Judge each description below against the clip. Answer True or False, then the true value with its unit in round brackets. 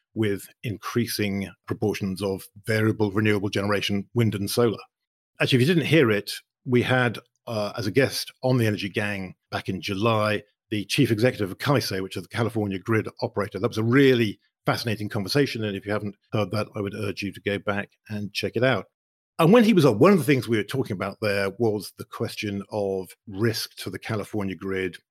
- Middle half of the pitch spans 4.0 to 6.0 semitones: False (2.8 semitones)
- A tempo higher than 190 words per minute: True (205 wpm)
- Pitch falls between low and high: False (105 Hz)